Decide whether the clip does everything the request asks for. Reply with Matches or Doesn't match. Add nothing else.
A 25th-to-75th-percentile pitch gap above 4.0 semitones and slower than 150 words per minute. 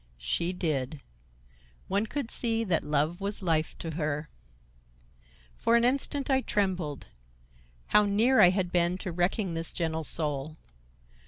Matches